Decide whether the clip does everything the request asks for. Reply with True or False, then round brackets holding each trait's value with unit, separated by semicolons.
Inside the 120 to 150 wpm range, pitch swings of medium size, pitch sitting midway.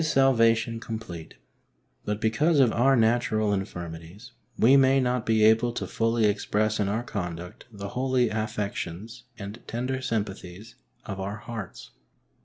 False (135 wpm; 3.1 semitones; 110 Hz)